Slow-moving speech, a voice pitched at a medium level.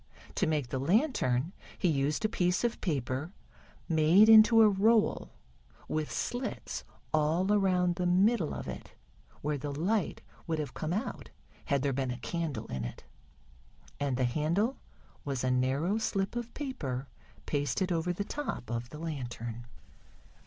No: average, 150 wpm; medium, 160 Hz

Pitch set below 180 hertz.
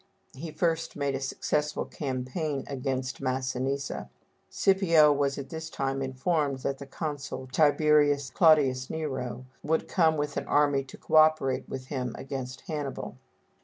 Yes: medium, 140 Hz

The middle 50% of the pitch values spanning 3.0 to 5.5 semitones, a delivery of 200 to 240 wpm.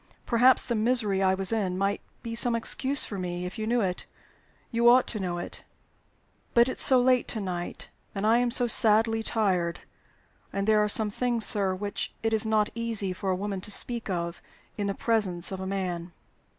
Yes: average, 3.6 semitones; fast, 205 wpm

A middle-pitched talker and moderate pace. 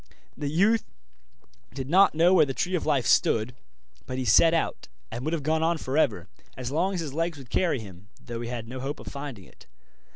No: medium, 145 Hz; fast, 225 wpm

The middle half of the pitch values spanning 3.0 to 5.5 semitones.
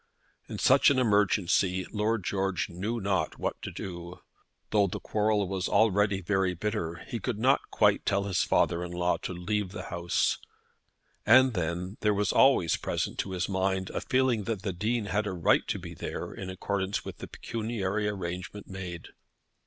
No: narrow, 2.6 semitones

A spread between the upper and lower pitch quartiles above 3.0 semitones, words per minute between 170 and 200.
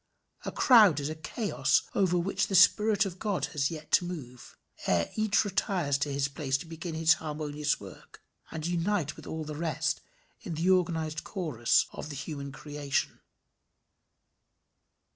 No: average, 3.8 semitones; average, 160 wpm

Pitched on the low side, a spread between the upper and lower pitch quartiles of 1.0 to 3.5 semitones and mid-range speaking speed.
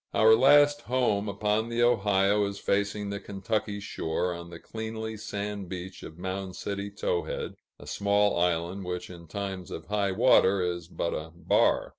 Yes: low, 100 Hz; average, 2.8 semitones; average, 165 wpm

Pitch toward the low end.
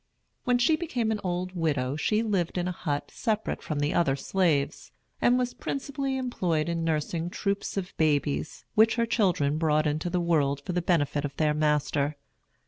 No: medium, 170 Hz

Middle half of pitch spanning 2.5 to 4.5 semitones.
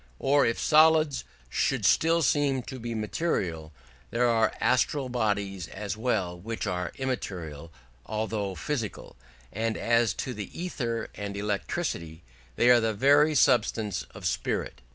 No: average, 4.9 semitones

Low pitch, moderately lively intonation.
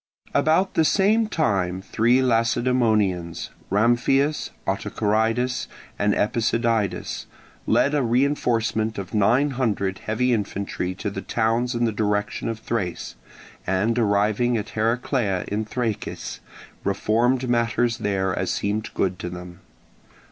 Yes: low, 110 Hz; average, 3.3 semitones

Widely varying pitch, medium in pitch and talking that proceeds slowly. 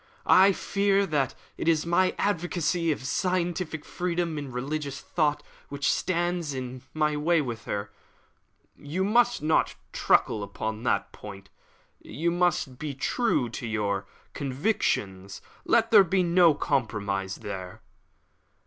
Yes: wide, 6.6 semitones; medium, 150 Hz; slow, 130 wpm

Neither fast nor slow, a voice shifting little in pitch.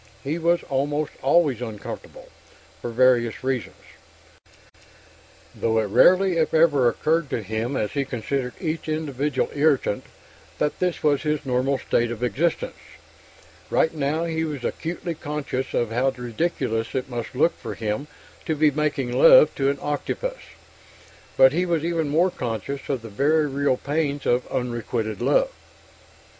No: average, 150 wpm; average, 4.3 semitones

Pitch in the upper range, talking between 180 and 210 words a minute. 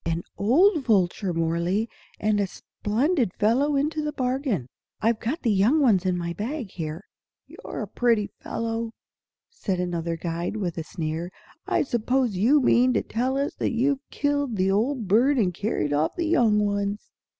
No: high, 220 Hz; average, 170 wpm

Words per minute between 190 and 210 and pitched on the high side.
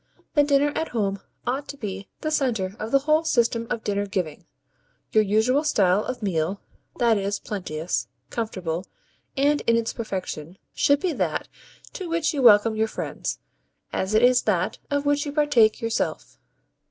No: average, 165 wpm; high, 225 Hz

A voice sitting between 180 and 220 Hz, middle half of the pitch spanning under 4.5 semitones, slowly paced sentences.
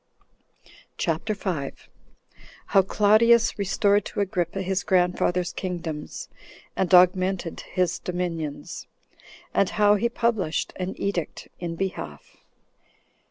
Yes: medium, 185 Hz; narrow, 2.6 semitones; slow, 100 wpm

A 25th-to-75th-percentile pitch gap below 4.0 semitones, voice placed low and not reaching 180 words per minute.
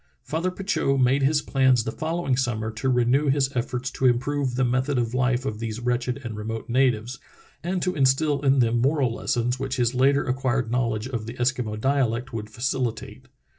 No: narrow, 2.4 semitones; low, 130 Hz; average, 190 wpm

